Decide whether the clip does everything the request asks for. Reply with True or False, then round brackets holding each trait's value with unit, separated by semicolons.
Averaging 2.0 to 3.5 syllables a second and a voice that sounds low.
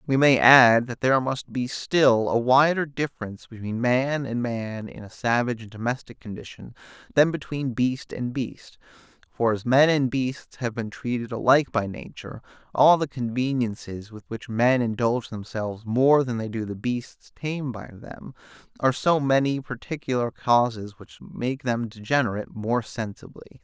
False (4.8 syllables/s; 125 Hz)